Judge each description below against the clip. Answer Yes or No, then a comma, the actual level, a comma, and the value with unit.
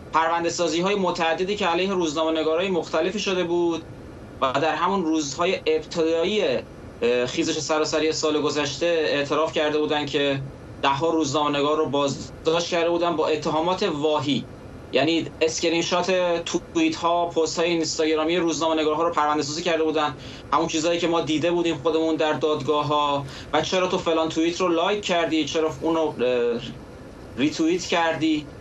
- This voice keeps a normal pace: Yes, average, 135 wpm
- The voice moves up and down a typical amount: No, narrow, 2.0 semitones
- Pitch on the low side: No, medium, 160 Hz